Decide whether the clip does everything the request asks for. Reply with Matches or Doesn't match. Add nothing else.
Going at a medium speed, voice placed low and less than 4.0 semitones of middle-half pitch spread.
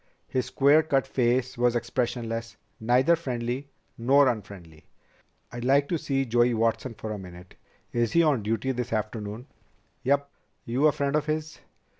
Matches